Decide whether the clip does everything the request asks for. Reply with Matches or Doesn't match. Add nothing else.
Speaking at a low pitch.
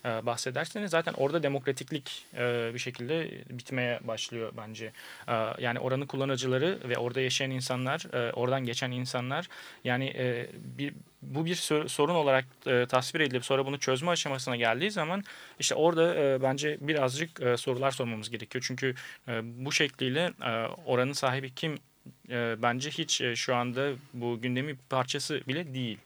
Matches